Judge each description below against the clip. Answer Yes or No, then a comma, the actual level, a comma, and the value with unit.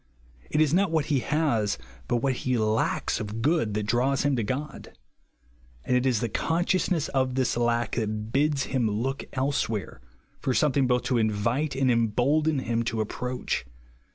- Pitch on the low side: Yes, low, 125 Hz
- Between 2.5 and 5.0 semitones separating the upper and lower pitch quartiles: Yes, average, 3.8 semitones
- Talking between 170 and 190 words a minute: Yes, average, 175 wpm